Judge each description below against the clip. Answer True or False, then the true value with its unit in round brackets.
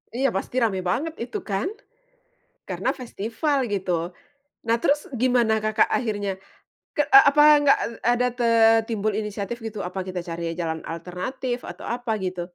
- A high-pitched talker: True (220 Hz)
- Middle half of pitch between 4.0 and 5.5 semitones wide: True (4.8 semitones)